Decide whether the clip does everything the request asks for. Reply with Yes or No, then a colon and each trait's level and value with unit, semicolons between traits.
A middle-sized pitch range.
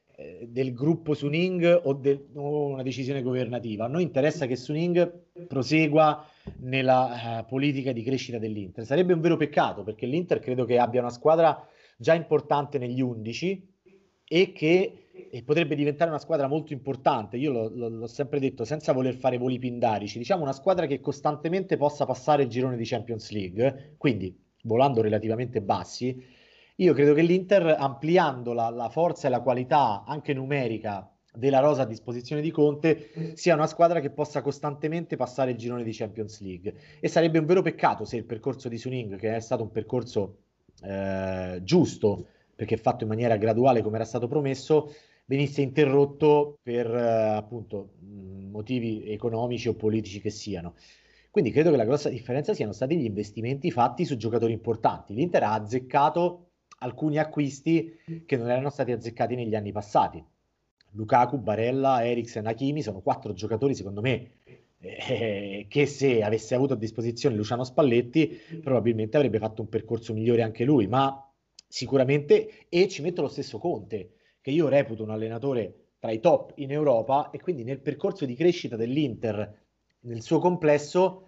Yes: average, 4.8 semitones